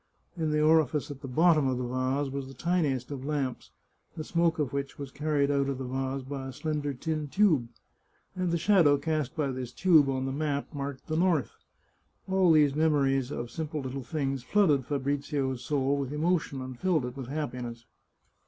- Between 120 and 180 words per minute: No, average, 190 wpm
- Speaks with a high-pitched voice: No, medium, 140 Hz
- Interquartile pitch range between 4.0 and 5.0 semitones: No, average, 2.8 semitones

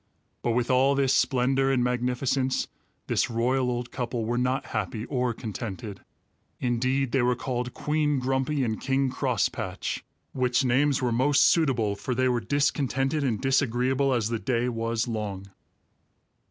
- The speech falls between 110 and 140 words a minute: No, average, 150 wpm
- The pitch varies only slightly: Yes, narrow, 2.1 semitones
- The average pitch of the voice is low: Yes, low, 125 Hz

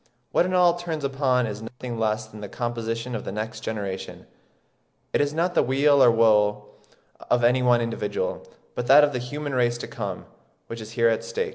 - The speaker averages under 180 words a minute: No, average, 200 wpm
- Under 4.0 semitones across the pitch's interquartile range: No, average, 4.3 semitones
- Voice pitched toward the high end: No, low, 120 Hz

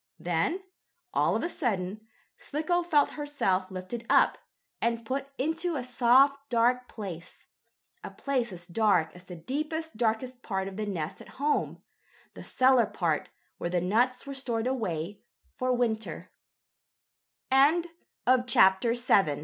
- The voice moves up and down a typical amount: No, wide, 6.6 semitones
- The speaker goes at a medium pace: No, slow, 120 wpm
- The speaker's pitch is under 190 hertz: No, high, 235 Hz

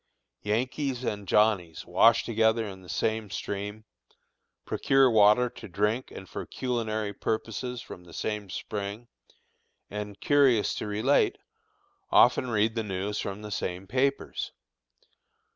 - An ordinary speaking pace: No, slow, 125 wpm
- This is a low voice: Yes, low, 110 Hz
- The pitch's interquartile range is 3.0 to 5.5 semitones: No, narrow, 2.6 semitones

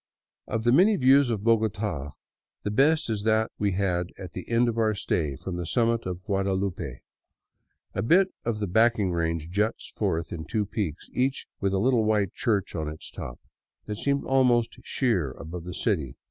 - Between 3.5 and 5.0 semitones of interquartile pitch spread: Yes, average, 4.7 semitones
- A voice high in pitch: No, low, 105 Hz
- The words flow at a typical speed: Yes, average, 185 wpm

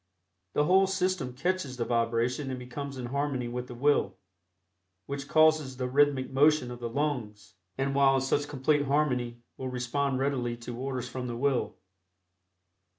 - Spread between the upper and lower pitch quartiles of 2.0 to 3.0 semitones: Yes, average, 2.7 semitones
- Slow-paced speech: No, average, 160 wpm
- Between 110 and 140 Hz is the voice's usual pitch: Yes, low, 135 Hz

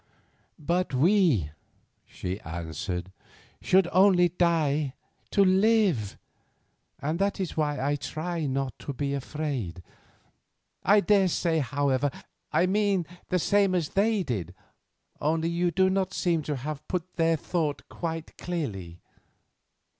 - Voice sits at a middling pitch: Yes, medium, 160 Hz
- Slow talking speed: Yes, slow, 125 wpm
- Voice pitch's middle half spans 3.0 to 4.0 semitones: No, average, 5.0 semitones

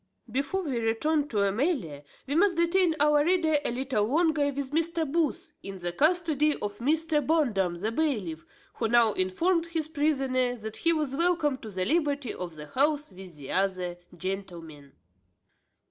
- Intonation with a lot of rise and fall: Yes, wide, 8.0 semitones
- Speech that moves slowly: No, average, 165 wpm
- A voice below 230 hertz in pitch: No, very high, 275 Hz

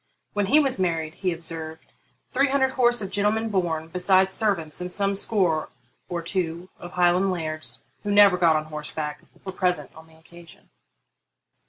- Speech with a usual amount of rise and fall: Yes, average, 3.8 semitones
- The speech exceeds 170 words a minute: No, average, 160 wpm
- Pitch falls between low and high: Yes, medium, 180 Hz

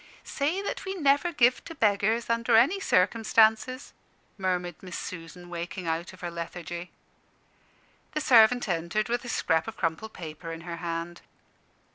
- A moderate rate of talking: Yes, average, 150 wpm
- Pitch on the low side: No, high, 190 Hz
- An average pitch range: No, wide, 6.0 semitones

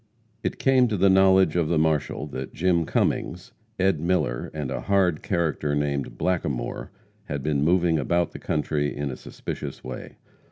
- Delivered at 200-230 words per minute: No, average, 165 wpm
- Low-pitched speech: Yes, very low, 80 Hz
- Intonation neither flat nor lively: Yes, average, 4.0 semitones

